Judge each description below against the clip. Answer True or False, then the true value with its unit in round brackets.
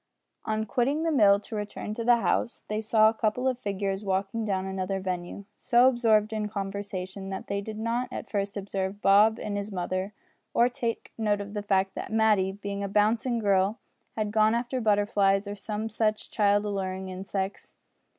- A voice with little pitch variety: True (2.0 semitones)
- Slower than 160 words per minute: False (185 wpm)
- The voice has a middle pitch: False (205 Hz)